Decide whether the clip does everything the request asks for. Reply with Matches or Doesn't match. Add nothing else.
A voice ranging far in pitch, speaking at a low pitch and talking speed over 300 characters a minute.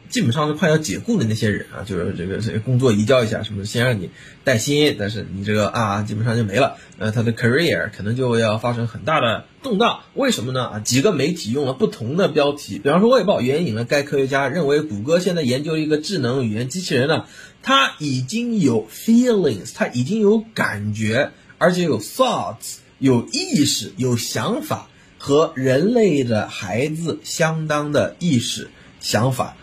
Matches